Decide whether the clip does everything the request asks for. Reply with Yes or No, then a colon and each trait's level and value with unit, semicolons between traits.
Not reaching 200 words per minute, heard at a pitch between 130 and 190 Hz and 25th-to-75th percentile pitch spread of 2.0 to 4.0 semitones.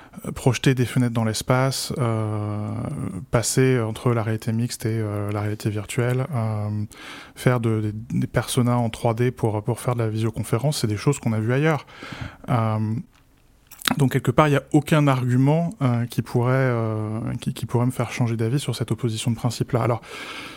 No: average, 185 wpm; low, 120 Hz; narrow, 2.6 semitones